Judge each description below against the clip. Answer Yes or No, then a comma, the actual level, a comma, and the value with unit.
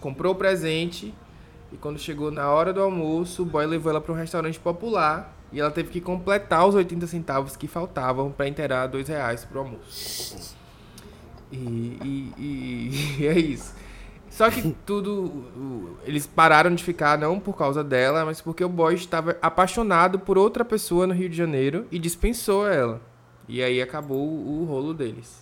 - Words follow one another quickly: No, average, 175 wpm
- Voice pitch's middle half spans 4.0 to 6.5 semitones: Yes, average, 4.6 semitones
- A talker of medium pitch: Yes, medium, 160 Hz